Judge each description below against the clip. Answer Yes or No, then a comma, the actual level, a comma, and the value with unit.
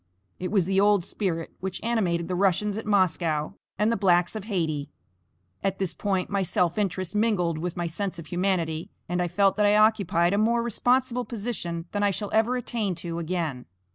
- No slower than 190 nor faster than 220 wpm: Yes, average, 195 wpm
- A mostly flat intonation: No, average, 3.5 semitones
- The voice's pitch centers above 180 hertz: Yes, high, 190 Hz